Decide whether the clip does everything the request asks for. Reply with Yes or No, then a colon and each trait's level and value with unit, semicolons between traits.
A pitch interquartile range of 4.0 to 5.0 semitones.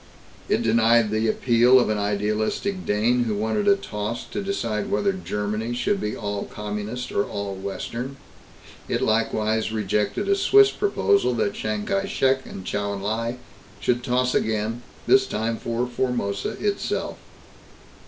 No: average, 3.6 semitones